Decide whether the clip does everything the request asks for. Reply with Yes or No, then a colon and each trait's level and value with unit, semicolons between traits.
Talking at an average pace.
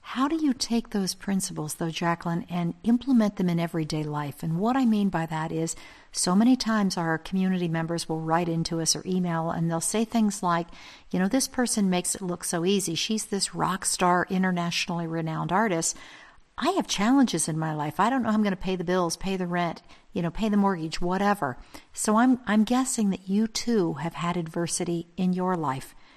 No: fast, 210 wpm